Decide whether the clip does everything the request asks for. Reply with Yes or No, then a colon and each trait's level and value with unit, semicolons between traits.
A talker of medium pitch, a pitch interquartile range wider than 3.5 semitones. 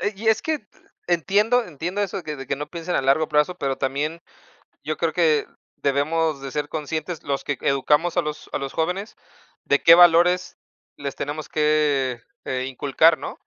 Yes: medium, 155 Hz; average, 4.0 semitones